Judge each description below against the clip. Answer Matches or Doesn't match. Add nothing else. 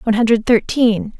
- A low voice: Doesn't match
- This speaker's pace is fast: Doesn't match